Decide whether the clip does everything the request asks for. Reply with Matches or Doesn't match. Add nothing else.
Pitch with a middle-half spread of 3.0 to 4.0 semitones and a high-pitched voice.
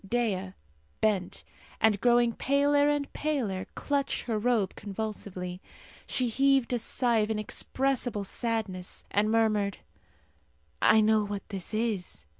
Matches